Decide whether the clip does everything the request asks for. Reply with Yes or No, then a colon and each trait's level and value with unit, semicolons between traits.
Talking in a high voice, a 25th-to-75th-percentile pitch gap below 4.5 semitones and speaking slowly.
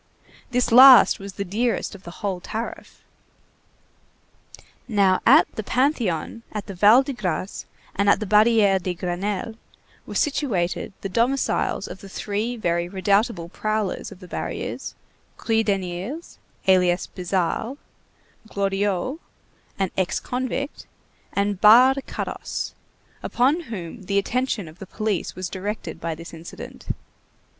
Yes: high, 200 Hz; average, 3.9 semitones; slow, 130 wpm